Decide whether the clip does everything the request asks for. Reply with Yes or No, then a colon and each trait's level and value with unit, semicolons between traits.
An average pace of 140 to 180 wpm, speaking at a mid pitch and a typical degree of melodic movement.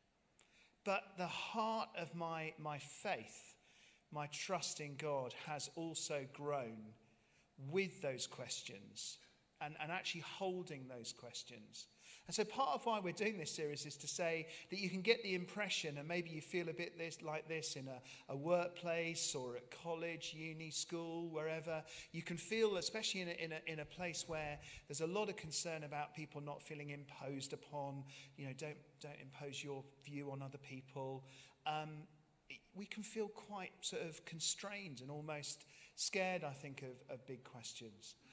Yes: average, 170 wpm; medium, 155 Hz; average, 3.3 semitones